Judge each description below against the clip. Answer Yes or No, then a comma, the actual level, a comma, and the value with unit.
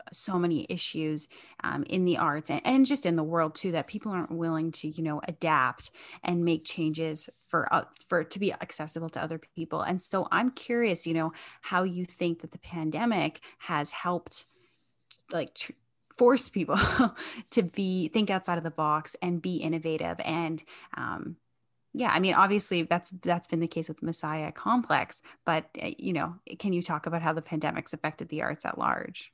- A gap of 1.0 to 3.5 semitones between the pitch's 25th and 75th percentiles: Yes, narrow, 2.4 semitones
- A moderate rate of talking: Yes, average, 190 wpm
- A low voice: No, medium, 170 Hz